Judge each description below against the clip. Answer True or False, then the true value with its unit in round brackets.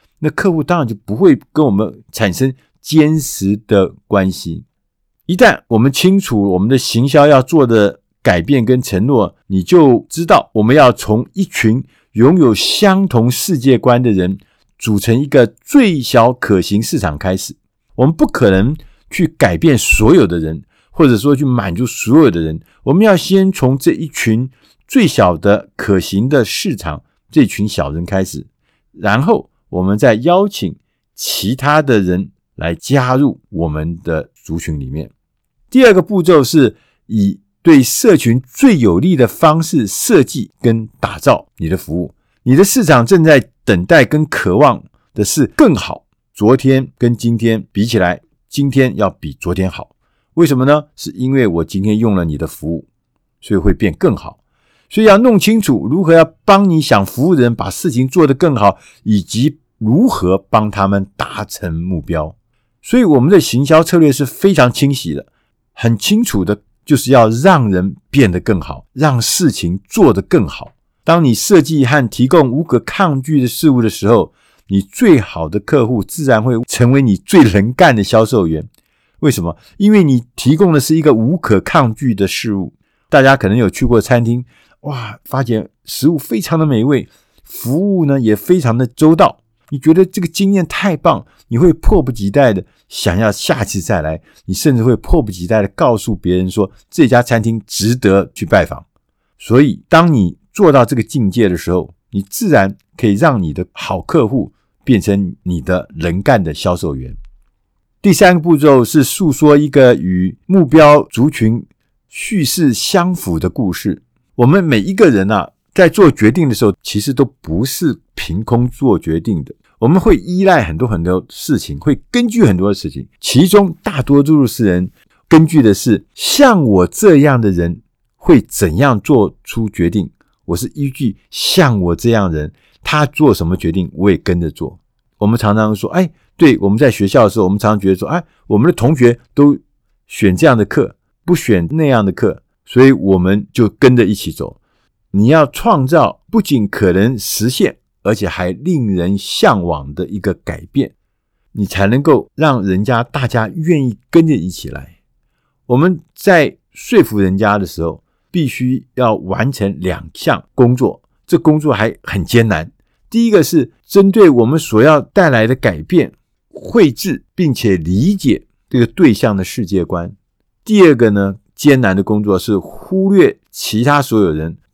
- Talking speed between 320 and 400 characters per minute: False (245 characters per minute)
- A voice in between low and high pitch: False (115 Hz)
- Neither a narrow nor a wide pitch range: False (7.0 semitones)